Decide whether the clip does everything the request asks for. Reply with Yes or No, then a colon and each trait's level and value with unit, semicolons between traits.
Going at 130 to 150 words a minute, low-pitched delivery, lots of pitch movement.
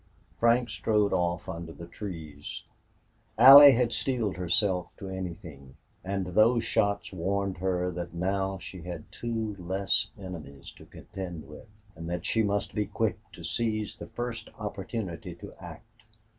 No: average, 145 wpm; very low, 95 Hz; average, 3.7 semitones